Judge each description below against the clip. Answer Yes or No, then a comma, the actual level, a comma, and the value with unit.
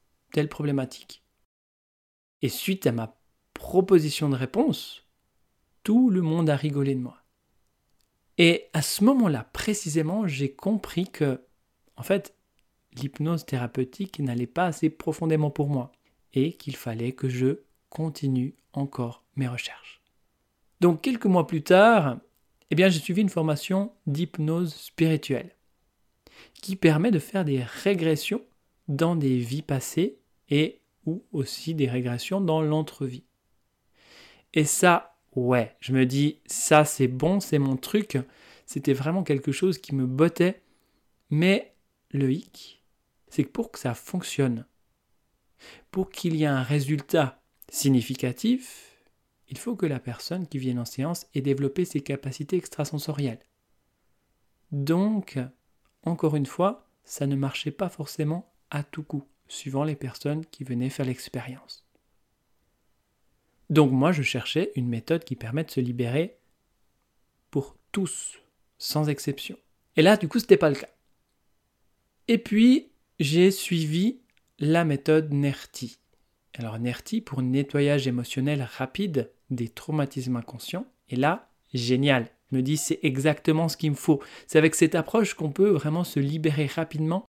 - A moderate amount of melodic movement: Yes, average, 4.5 semitones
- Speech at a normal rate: No, slow, 140 wpm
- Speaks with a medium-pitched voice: Yes, medium, 150 Hz